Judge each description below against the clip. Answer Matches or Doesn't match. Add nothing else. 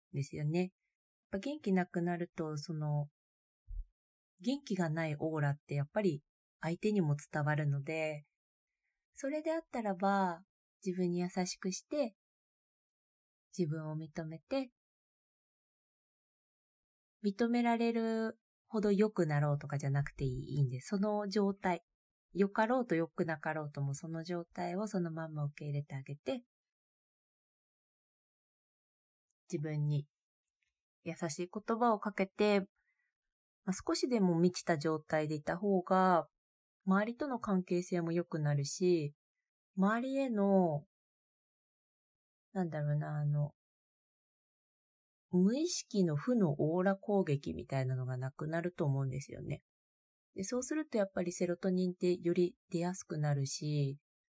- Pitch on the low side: Doesn't match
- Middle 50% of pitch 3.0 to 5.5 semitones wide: Matches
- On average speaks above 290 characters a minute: Doesn't match